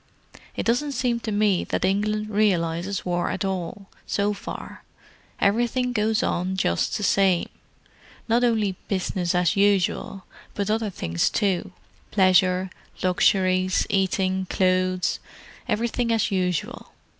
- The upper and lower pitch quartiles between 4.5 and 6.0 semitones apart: No, narrow, 2.5 semitones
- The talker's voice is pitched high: Yes, high, 195 Hz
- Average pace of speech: No, slow, 120 wpm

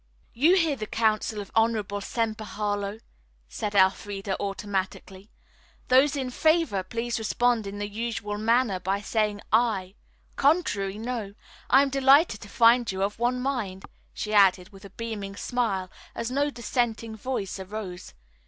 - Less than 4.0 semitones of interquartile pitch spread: Yes, average, 3.4 semitones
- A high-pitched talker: Yes, high, 215 Hz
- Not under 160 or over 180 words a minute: No, average, 145 wpm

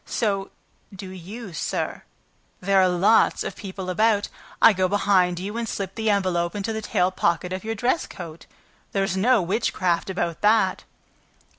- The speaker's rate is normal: Yes, average, 160 wpm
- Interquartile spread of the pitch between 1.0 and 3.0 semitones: Yes, narrow, 2.6 semitones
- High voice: Yes, high, 195 Hz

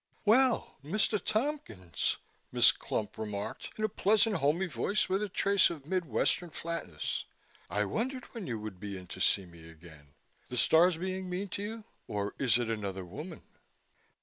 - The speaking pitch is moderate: Yes, medium, 165 Hz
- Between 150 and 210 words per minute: Yes, average, 170 wpm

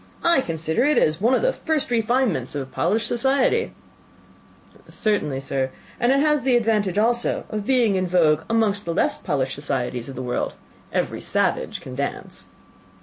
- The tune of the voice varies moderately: No, wide, 8.8 semitones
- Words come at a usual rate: Yes, average, 165 wpm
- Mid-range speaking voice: No, high, 210 Hz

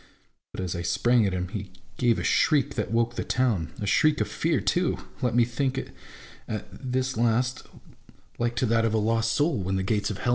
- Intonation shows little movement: No, average, 3.6 semitones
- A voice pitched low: Yes, low, 115 Hz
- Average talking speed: No, fast, 210 wpm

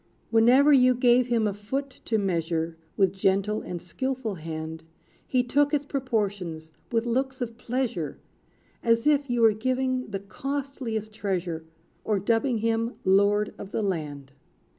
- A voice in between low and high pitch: No, high, 225 Hz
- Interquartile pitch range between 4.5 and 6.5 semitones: Yes, average, 4.9 semitones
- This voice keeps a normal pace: Yes, average, 145 wpm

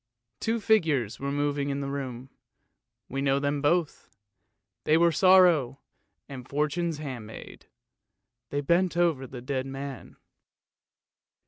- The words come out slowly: Yes, slow, 125 wpm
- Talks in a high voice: No, medium, 140 Hz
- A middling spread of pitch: Yes, average, 3.6 semitones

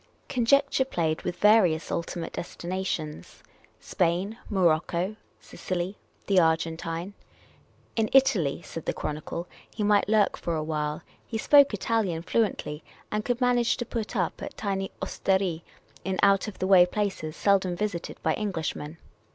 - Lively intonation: No, average, 4.2 semitones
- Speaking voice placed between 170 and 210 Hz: Yes, high, 190 Hz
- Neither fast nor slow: Yes, average, 145 wpm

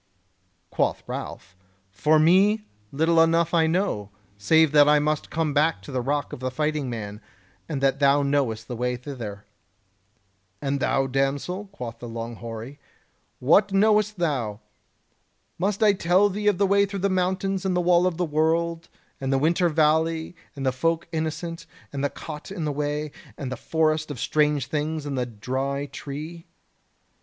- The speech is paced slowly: No, average, 170 wpm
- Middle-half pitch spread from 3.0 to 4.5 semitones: Yes, average, 4.1 semitones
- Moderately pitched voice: Yes, medium, 150 Hz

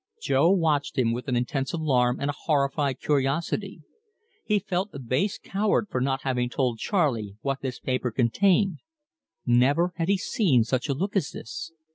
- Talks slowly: No, average, 170 wpm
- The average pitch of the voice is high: No, medium, 140 Hz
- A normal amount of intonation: No, wide, 5.9 semitones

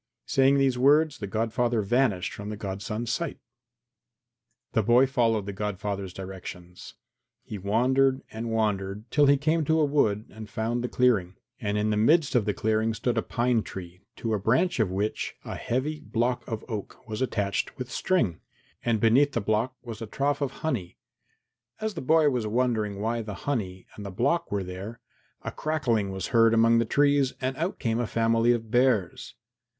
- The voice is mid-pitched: No, low, 115 Hz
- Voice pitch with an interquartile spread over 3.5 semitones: Yes, average, 4.0 semitones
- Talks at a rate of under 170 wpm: No, average, 185 wpm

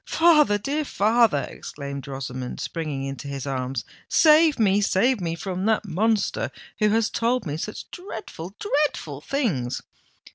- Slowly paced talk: Yes, slow, 120 wpm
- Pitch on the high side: Yes, high, 195 Hz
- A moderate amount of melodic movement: No, wide, 9.0 semitones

